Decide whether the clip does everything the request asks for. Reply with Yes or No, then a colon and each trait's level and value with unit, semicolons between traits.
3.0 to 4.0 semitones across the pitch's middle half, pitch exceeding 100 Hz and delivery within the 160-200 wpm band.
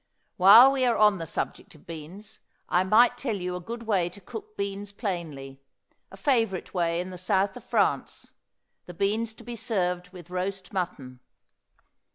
Yes: average, 3.6 semitones; high, 190 Hz; average, 175 wpm